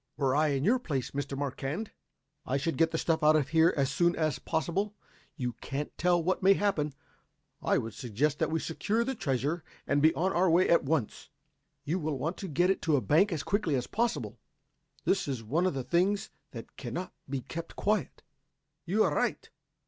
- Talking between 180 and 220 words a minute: Yes, average, 200 wpm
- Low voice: No, medium, 160 Hz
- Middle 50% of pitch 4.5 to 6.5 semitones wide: Yes, average, 4.8 semitones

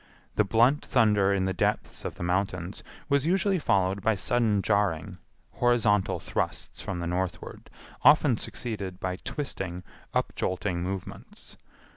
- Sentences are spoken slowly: Yes, slow, 130 wpm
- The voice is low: Yes, low, 100 Hz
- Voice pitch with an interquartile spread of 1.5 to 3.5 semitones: No, average, 4.3 semitones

